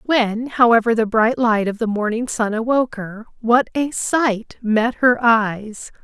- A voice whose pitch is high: Yes, high, 230 Hz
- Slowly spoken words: No, average, 170 wpm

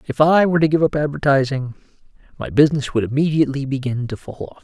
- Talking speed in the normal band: Yes, average, 195 wpm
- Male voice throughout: Yes, male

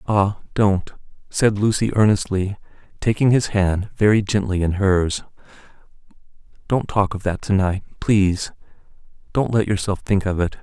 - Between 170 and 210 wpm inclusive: No, average, 140 wpm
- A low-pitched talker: Yes, low, 100 Hz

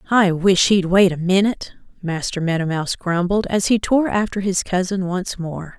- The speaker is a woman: Yes, female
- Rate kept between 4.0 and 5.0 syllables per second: Yes, 4.9 syllables/s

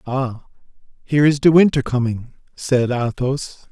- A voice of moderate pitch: No, low, 130 Hz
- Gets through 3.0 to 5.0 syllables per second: Yes, 4.5 syllables/s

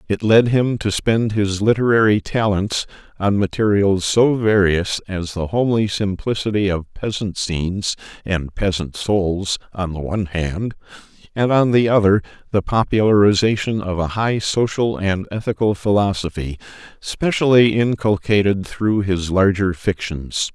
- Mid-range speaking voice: No, low, 100 Hz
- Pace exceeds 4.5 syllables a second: No, 4.4 syllables/s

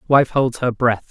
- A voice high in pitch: No, low, 125 Hz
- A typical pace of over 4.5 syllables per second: No, 4.2 syllables/s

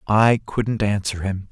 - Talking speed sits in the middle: Yes, average, 160 wpm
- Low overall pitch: Yes, low, 100 Hz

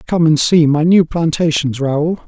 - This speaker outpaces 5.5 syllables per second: No, 4.3 syllables/s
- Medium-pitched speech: Yes, medium, 160 Hz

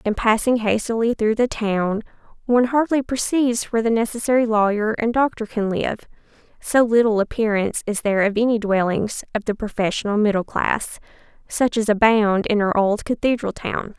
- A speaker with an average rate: Yes, average, 165 wpm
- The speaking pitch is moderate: No, high, 220 Hz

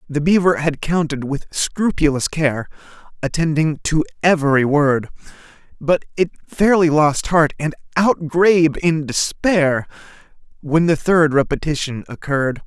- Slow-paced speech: Yes, slow, 120 wpm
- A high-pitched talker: No, medium, 155 Hz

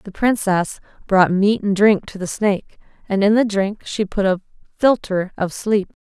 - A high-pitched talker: Yes, high, 200 Hz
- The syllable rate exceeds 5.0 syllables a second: No, 4.5 syllables/s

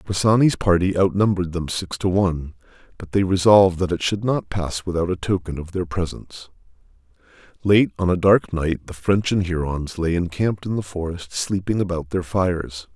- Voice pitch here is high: No, very low, 90 Hz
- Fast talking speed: No, average, 180 wpm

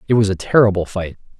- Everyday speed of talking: No, fast, 215 wpm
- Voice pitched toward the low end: Yes, low, 100 Hz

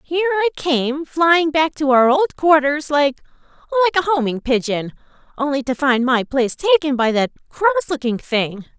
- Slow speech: No, average, 165 wpm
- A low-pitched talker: No, very high, 290 Hz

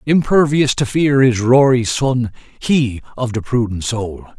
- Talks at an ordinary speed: Yes, average, 150 wpm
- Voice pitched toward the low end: Yes, low, 125 Hz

